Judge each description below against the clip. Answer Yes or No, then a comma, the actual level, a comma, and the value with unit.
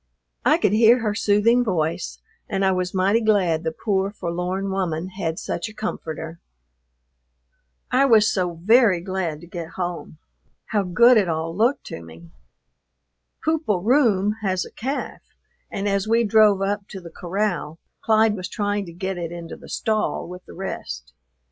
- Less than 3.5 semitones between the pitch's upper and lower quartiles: No, average, 3.8 semitones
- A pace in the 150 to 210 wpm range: Yes, average, 165 wpm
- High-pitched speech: Yes, high, 195 Hz